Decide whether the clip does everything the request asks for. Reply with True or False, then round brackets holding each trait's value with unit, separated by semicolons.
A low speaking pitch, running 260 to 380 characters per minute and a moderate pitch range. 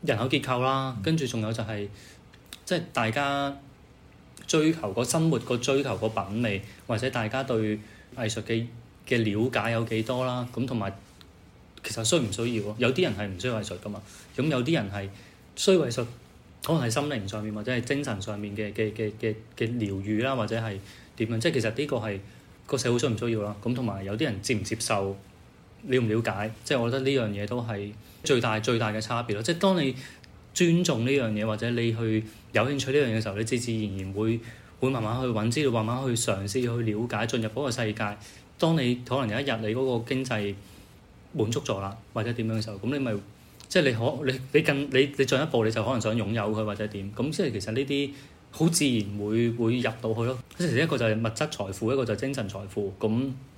True (115 Hz; 310 characters per minute; 3.6 semitones)